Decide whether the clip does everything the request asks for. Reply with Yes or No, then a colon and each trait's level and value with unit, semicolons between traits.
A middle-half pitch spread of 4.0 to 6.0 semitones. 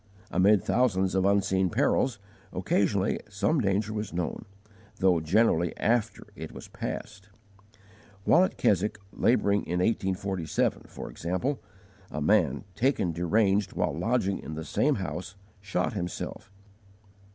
No: average, 3.0 semitones